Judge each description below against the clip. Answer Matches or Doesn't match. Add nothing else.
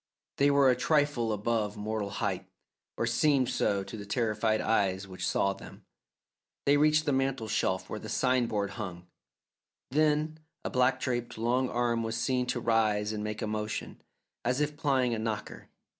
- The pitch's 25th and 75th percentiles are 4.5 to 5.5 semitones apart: Doesn't match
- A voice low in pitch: Matches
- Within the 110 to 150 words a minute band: Doesn't match